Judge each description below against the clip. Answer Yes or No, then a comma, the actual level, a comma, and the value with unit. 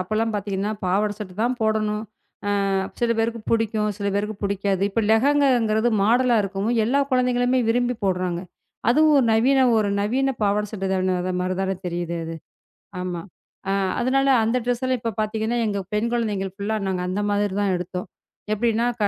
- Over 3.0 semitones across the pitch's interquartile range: Yes, average, 3.5 semitones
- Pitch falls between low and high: No, high, 215 Hz